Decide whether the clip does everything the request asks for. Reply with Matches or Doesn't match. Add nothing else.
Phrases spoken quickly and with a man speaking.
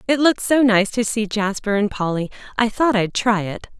Doesn't match